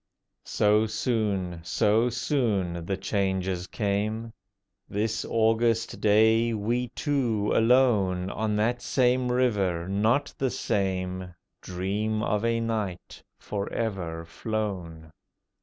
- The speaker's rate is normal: No, slow, 105 wpm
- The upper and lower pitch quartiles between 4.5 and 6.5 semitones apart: No, average, 3.3 semitones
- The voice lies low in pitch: Yes, low, 105 Hz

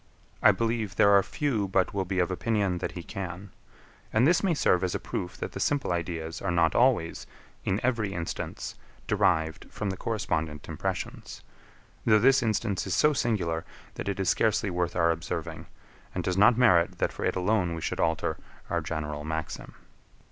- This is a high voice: No, very low, 95 Hz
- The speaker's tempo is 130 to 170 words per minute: No, average, 185 wpm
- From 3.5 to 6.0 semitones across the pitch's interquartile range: Yes, average, 4.4 semitones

